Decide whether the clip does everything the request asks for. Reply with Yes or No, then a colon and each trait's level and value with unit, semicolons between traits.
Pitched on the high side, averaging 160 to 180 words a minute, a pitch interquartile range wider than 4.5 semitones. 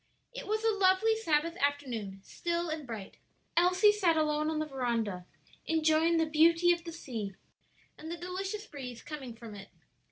Yes: very high, 315 Hz; average, 165 wpm; wide, 5.6 semitones